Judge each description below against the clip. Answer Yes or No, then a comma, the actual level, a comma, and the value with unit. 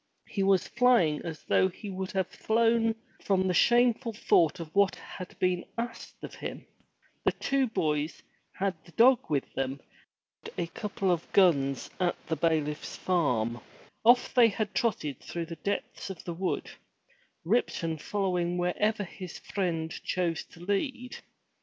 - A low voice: No, medium, 185 Hz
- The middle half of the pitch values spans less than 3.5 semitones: No, average, 4.7 semitones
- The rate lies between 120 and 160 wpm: Yes, average, 155 wpm